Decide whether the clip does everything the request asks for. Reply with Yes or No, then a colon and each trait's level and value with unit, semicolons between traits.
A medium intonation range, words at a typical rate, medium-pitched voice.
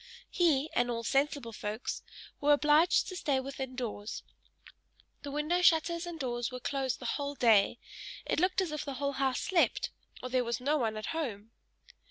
No: average, 4.0 semitones; average, 180 wpm; very high, 275 Hz